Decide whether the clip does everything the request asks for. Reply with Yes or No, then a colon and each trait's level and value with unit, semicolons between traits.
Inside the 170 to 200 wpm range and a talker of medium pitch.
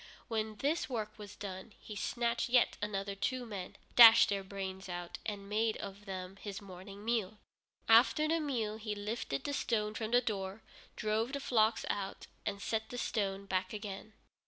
No: average, 175 wpm; high, 210 Hz